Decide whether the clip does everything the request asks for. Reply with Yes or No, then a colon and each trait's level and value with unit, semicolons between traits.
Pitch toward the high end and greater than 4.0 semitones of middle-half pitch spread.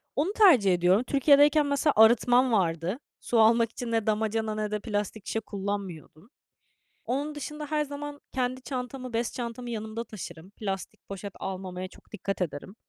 Yes: high, 225 Hz; average, 4.6 semitones